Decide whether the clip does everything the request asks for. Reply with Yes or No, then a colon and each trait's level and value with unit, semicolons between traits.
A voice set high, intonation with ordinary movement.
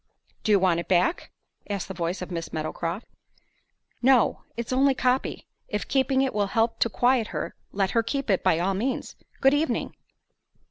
No: high, 215 Hz; wide, 5.7 semitones